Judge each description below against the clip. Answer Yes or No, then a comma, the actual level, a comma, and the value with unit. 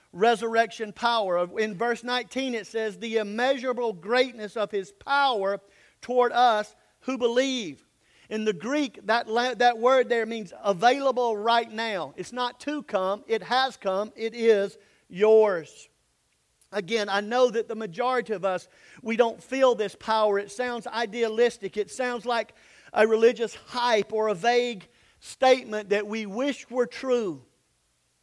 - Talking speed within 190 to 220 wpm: No, average, 150 wpm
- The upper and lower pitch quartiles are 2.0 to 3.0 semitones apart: Yes, average, 2.7 semitones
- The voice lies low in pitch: No, high, 230 Hz